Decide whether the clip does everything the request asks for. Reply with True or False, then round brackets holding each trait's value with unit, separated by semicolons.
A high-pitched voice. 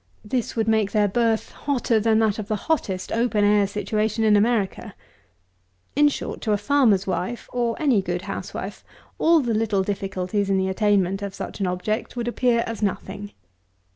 True (215 Hz)